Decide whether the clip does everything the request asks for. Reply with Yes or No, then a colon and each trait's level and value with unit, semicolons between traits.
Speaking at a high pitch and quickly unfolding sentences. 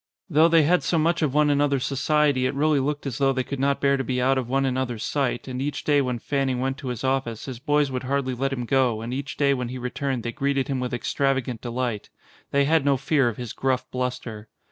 No: low, 135 Hz; fast, 255 wpm